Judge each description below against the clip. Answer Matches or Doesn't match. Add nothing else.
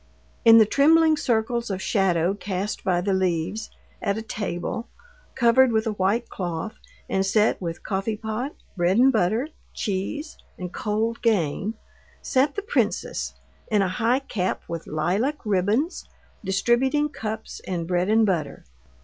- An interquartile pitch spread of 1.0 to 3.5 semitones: Doesn't match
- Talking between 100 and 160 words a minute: Matches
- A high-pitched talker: Matches